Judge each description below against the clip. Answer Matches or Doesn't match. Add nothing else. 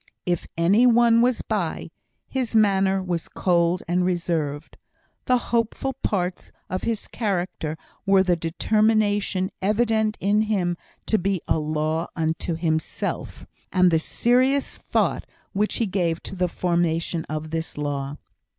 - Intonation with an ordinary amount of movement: Matches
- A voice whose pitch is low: Doesn't match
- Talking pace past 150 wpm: Doesn't match